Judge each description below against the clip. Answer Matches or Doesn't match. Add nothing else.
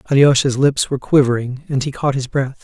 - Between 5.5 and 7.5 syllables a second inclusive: Matches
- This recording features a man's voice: Matches